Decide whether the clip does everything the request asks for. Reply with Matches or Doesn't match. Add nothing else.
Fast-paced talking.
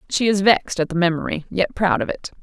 Matches